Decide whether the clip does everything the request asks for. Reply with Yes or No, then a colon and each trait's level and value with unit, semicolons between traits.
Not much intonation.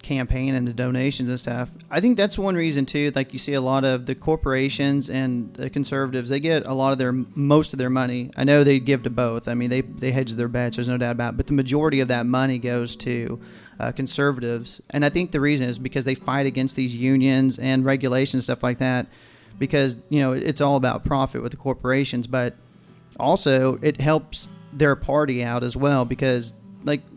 Yes: narrow, 2.1 semitones